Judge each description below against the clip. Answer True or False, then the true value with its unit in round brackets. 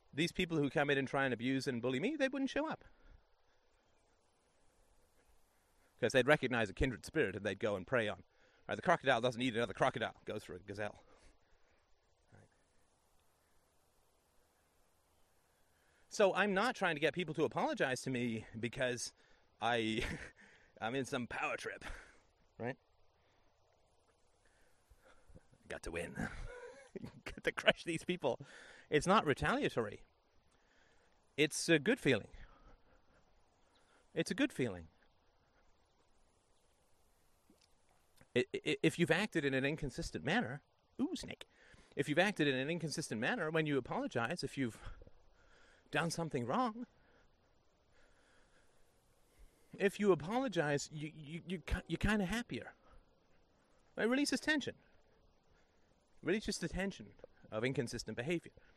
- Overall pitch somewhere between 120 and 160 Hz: True (135 Hz)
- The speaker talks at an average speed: False (125 wpm)